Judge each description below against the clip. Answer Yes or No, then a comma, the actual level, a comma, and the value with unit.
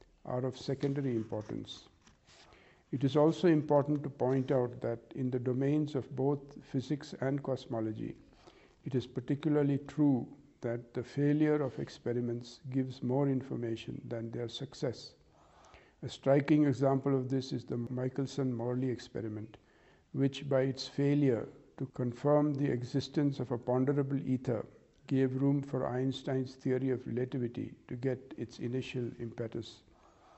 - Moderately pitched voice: No, low, 130 Hz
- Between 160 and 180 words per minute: No, slow, 135 wpm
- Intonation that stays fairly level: Yes, narrow, 2.3 semitones